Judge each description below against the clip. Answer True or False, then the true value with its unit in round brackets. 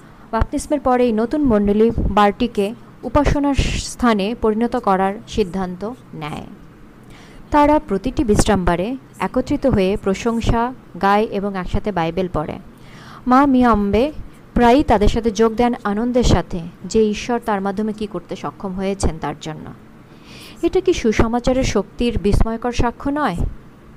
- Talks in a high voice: True (220 Hz)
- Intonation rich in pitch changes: False (4.0 semitones)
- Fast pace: True (125 wpm)